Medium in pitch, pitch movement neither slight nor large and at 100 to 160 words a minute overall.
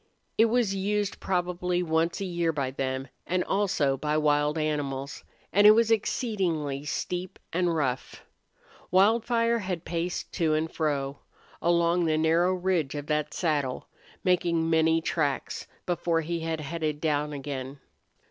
Yes: medium, 165 Hz; average, 3.5 semitones; average, 140 wpm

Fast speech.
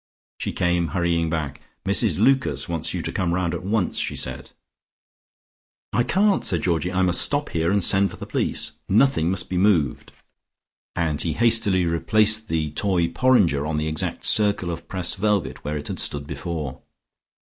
No: average, 175 wpm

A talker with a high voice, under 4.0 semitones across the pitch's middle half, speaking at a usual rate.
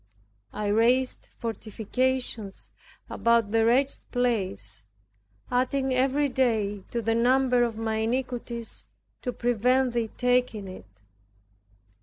No: high, 235 Hz; narrow, 2.4 semitones; slow, 105 wpm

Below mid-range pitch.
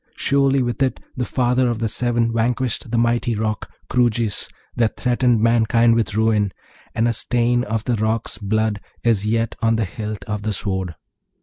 Yes: low, 115 Hz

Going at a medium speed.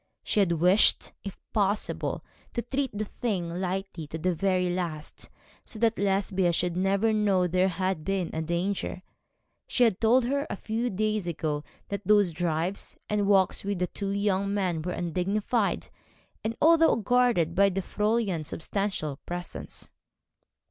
Yes: average, 150 wpm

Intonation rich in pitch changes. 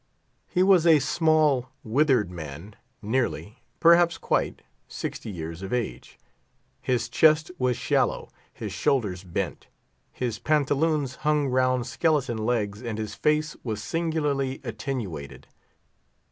Yes: wide, 6.0 semitones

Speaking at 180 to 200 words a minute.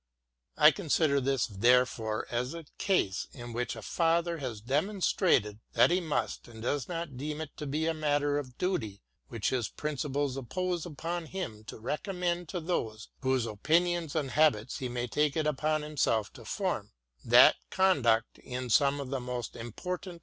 No: average, 165 wpm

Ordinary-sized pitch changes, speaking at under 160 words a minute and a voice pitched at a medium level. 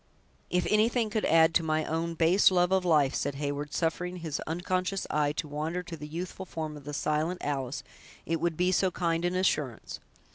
No: average, 3.0 semitones; average, 195 wpm; medium, 165 Hz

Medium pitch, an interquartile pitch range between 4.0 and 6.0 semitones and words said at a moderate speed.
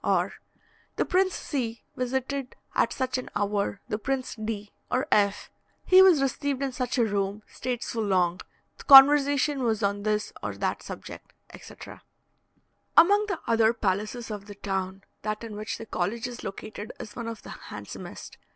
No: high, 230 Hz; average, 4.5 semitones; average, 170 wpm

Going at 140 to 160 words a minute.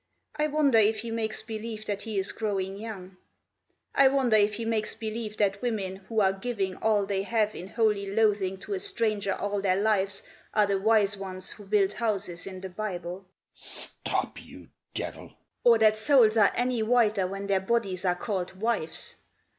No: average, 185 wpm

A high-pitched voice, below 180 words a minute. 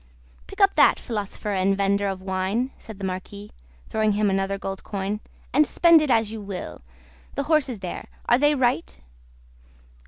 Yes: high, 205 Hz; average, 165 wpm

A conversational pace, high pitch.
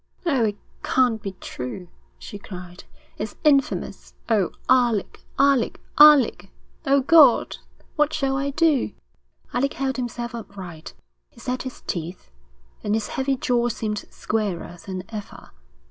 No: slow, 130 wpm; high, 235 Hz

